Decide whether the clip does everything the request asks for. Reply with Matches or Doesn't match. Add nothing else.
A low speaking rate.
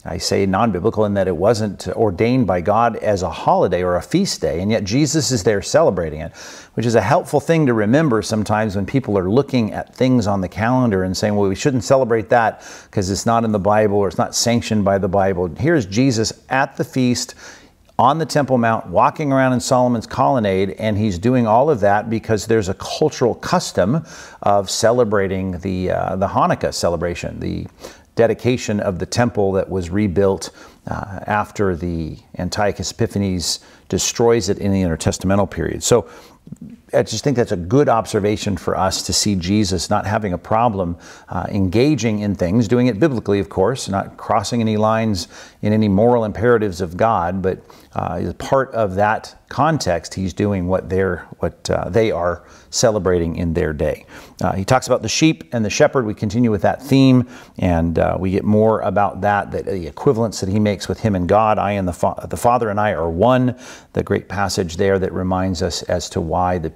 Doesn't match